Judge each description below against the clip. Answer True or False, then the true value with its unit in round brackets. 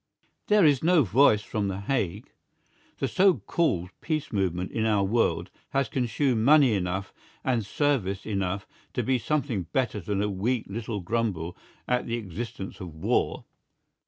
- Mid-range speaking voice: False (110 Hz)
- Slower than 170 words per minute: True (155 wpm)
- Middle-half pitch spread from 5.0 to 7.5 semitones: True (5.3 semitones)